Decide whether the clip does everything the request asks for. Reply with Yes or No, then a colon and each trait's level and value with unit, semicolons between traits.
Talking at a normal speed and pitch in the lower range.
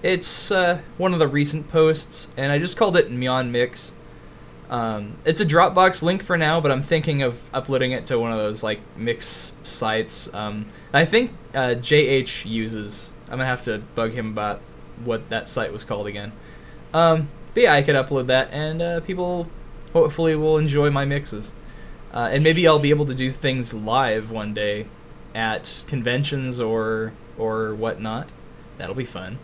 Yes: average, 180 wpm; low, 130 Hz